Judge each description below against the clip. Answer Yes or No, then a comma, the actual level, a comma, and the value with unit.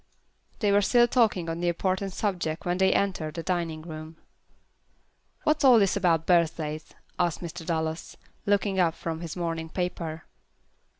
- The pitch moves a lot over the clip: No, average, 3.0 semitones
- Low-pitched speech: No, medium, 175 Hz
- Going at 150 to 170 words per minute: Yes, average, 155 wpm